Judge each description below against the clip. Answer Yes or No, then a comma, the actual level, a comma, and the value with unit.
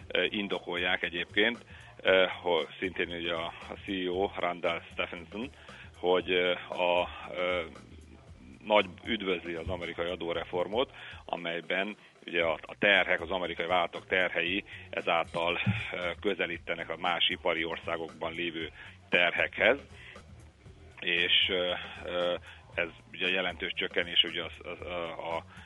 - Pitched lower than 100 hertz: Yes, very low, 90 Hz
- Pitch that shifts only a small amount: Yes, narrow, 1.7 semitones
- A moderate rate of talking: No, slow, 100 wpm